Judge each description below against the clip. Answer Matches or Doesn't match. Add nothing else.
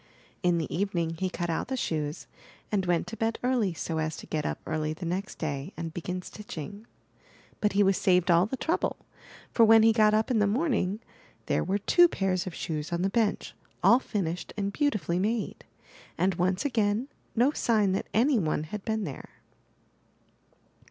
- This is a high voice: Matches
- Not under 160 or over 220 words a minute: Matches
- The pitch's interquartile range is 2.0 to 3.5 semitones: Doesn't match